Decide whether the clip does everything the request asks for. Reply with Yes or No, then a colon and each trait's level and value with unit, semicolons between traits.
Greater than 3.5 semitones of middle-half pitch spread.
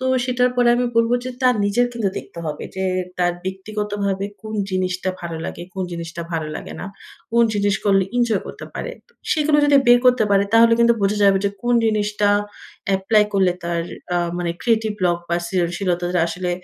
Yes: average, 4.2 semitones